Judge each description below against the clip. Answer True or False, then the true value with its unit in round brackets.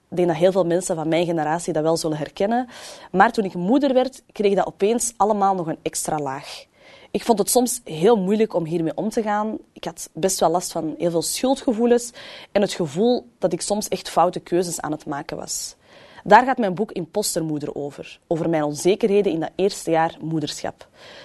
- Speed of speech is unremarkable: False (205 wpm)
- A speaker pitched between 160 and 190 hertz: True (185 Hz)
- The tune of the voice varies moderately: True (4.6 semitones)